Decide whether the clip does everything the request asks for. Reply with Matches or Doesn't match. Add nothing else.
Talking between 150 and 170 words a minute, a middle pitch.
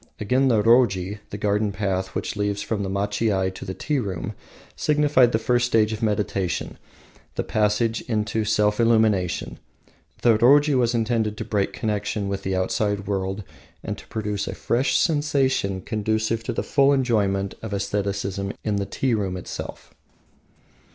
Doesn't match